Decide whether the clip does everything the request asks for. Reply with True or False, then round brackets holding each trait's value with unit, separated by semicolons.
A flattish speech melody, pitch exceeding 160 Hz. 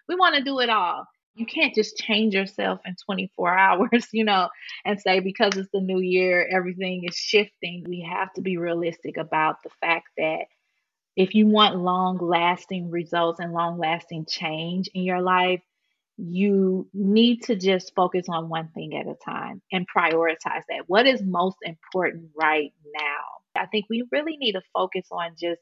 False (3.3 semitones; 185 Hz)